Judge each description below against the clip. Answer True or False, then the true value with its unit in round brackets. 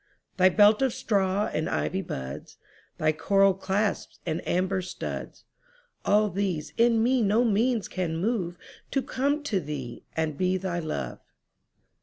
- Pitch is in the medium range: False (195 Hz)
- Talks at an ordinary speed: False (130 wpm)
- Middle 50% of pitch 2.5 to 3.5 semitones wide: False (4.3 semitones)